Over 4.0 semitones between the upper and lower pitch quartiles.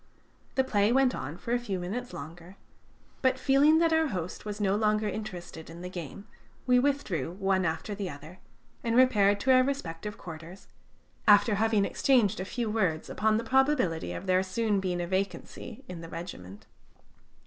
Yes: wide, 5.5 semitones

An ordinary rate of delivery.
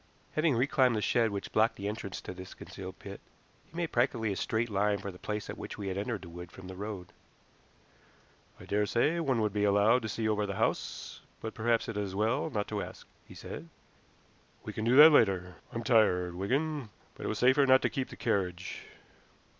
No: fast, 215 wpm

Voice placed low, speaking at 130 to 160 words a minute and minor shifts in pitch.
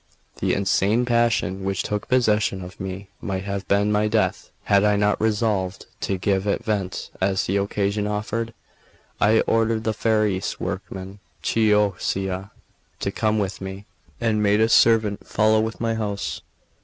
Yes: low, 105 Hz; average, 155 wpm; narrow, 2.0 semitones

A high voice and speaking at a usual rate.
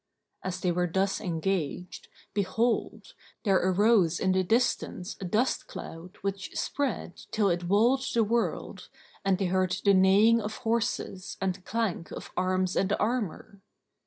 Yes: high, 195 Hz; average, 145 wpm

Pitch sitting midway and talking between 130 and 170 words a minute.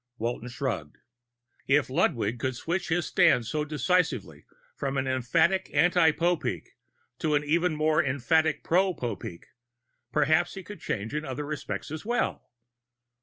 Yes: medium, 150 Hz; average, 140 wpm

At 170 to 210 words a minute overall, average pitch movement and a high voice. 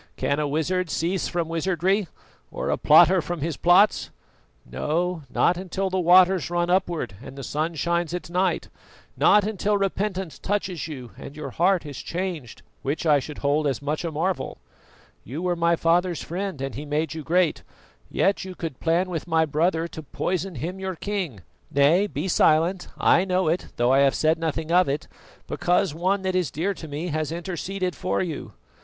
No: average, 185 wpm; average, 3.2 semitones; medium, 170 Hz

